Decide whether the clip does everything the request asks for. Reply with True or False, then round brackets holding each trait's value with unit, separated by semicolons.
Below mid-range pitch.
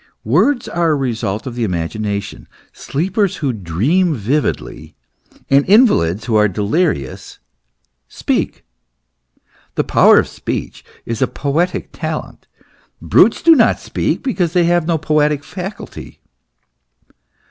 False (145 Hz)